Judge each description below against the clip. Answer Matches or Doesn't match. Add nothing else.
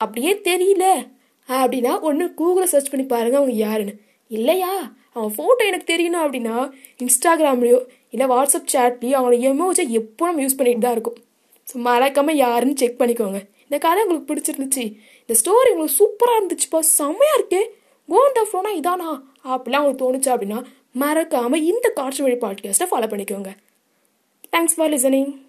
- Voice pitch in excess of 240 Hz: Matches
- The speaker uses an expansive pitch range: Matches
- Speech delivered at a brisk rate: Matches